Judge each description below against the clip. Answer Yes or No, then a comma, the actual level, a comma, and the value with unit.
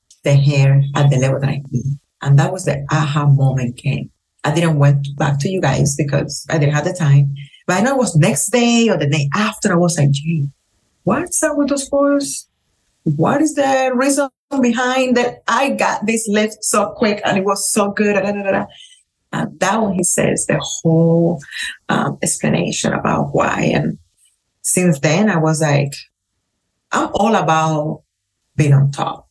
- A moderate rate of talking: Yes, average, 180 wpm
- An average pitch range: No, wide, 7.1 semitones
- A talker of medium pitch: Yes, medium, 160 Hz